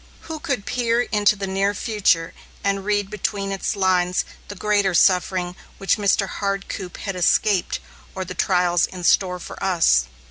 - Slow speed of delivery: No, average, 155 wpm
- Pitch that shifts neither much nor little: No, narrow, 2.1 semitones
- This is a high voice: Yes, high, 195 Hz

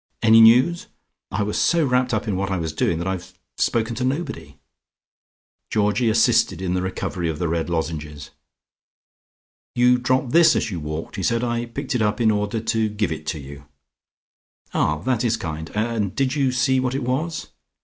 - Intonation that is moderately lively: No, wide, 6.0 semitones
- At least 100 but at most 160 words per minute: No, average, 185 wpm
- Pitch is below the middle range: Yes, low, 110 Hz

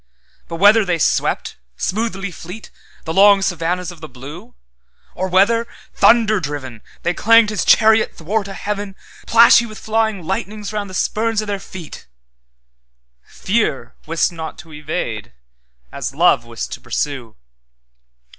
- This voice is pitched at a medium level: Yes, medium, 180 Hz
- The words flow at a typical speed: No, slow, 125 wpm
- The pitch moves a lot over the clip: Yes, wide, 6.8 semitones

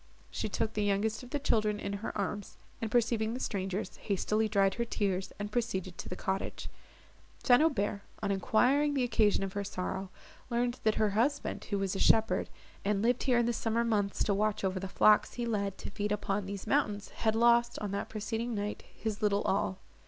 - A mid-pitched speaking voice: No, high, 210 Hz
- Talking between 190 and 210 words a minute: Yes, fast, 205 wpm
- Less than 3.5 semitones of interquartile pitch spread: Yes, narrow, 2.6 semitones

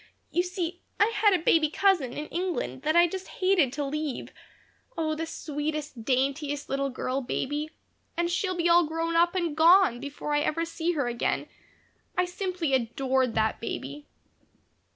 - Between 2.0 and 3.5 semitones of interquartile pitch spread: No, average, 4.1 semitones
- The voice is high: Yes, very high, 315 Hz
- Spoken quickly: No, average, 165 wpm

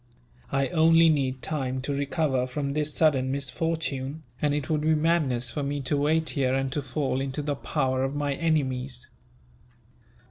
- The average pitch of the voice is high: No, medium, 140 Hz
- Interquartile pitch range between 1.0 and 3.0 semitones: Yes, average, 2.7 semitones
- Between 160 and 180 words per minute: Yes, average, 170 wpm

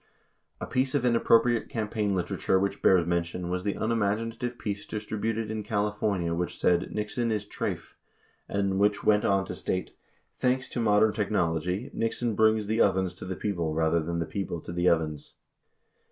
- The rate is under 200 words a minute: Yes, average, 170 wpm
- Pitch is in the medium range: No, low, 100 Hz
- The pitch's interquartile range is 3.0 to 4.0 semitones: Yes, average, 3.6 semitones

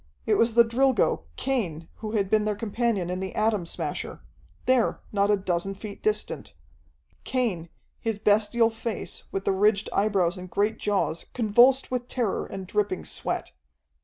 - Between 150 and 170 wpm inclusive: Yes, average, 160 wpm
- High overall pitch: Yes, high, 210 Hz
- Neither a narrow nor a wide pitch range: Yes, average, 3.1 semitones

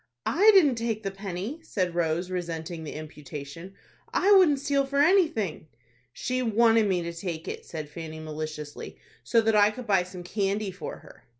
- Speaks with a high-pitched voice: Yes, high, 195 Hz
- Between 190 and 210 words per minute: No, average, 175 wpm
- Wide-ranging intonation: Yes, wide, 6.2 semitones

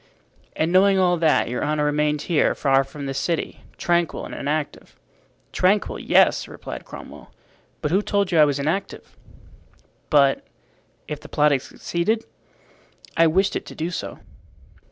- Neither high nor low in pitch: Yes, medium, 155 Hz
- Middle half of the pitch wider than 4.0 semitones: No, average, 3.7 semitones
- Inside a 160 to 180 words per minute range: No, average, 150 wpm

